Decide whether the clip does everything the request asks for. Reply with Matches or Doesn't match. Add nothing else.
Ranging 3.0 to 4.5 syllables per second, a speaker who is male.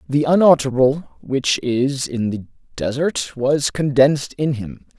Matches